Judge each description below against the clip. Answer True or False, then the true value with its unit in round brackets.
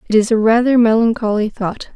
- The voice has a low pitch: False (220 Hz)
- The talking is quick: False (185 wpm)